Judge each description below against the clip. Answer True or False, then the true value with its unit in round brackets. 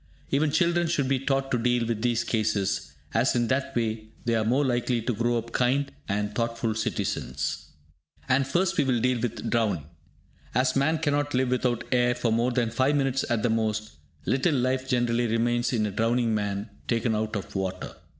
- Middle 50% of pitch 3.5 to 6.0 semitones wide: False (2.8 semitones)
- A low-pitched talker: True (120 Hz)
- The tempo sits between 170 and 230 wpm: True (195 wpm)